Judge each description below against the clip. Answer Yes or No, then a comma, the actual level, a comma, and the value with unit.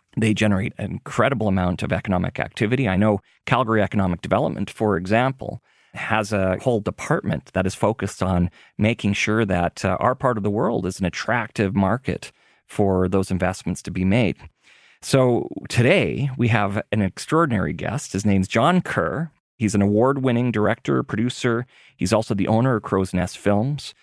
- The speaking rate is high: No, average, 165 wpm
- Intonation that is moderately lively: Yes, average, 3.8 semitones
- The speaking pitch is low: Yes, low, 105 Hz